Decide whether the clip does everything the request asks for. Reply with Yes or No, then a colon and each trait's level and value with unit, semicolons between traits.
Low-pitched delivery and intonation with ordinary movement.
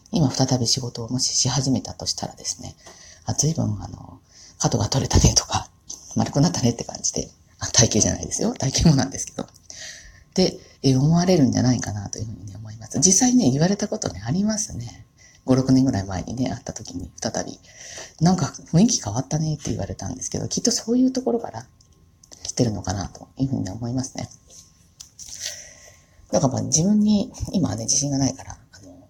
No: low, 125 Hz; wide, 6.7 semitones